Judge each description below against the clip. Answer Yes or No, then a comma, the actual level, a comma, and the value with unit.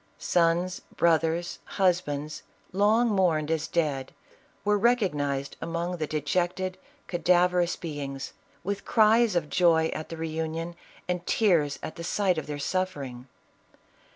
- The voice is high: No, medium, 170 Hz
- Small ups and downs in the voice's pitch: No, average, 3.1 semitones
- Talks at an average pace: No, slow, 125 wpm